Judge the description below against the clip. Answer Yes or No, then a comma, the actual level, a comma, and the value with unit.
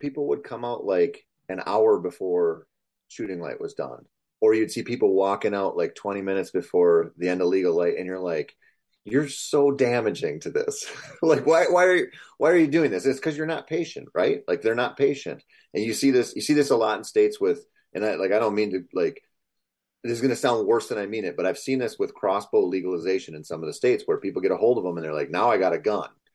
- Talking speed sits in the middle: No, fast, 255 wpm